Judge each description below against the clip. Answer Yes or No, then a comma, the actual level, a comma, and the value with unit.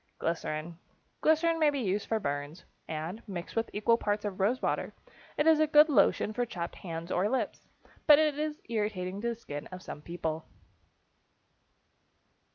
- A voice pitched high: Yes, high, 210 Hz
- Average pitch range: No, wide, 7.5 semitones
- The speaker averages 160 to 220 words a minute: Yes, average, 165 wpm